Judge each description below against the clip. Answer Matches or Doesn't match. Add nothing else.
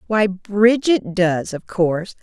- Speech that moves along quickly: Doesn't match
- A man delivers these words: Doesn't match